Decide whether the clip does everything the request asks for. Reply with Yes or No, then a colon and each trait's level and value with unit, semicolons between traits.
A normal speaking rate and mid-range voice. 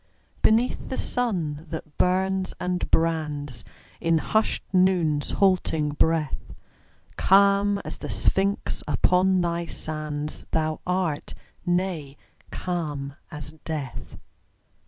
No: slow, 100 wpm; medium, 165 Hz